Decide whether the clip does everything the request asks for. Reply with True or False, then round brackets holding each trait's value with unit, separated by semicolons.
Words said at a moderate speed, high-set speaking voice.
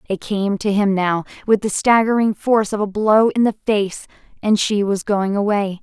True (195 wpm; 205 Hz)